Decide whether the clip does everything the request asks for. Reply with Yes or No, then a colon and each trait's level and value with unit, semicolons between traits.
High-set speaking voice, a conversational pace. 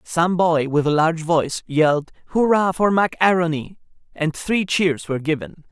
No: medium, 165 Hz; average, 170 wpm